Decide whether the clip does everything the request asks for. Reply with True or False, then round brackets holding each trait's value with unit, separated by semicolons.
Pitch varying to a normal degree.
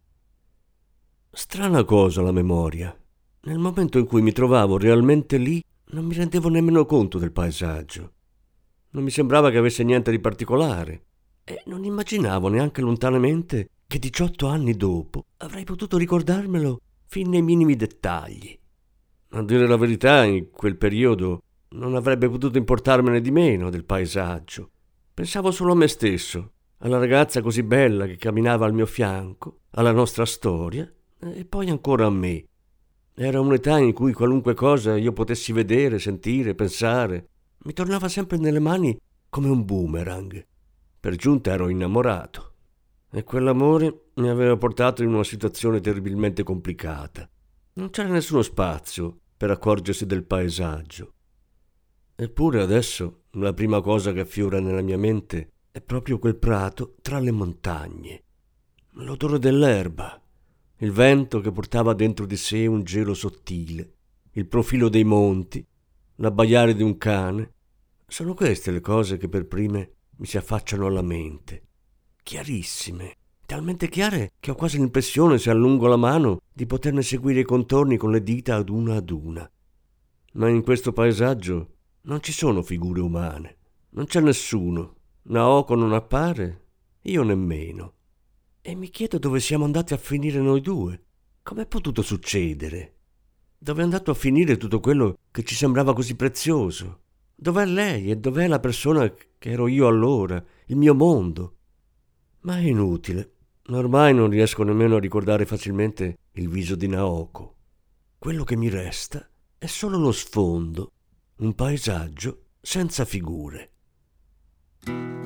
False (6.7 semitones)